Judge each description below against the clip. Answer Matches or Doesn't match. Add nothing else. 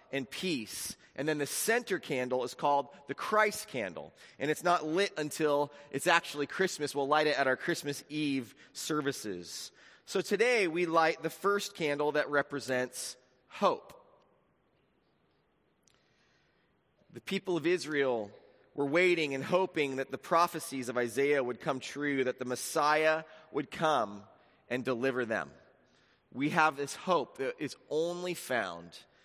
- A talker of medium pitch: Matches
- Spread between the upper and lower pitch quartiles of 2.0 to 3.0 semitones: Doesn't match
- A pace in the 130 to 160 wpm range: Matches